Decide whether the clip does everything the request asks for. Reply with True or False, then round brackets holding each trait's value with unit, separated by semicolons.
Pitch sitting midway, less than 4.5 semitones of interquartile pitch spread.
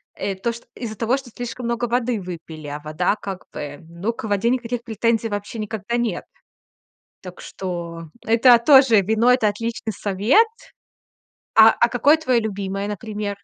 False (220 Hz; 3.4 semitones)